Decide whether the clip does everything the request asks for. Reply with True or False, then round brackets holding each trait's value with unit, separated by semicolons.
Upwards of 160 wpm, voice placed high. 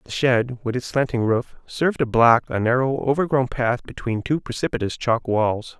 False (185 wpm; 125 Hz)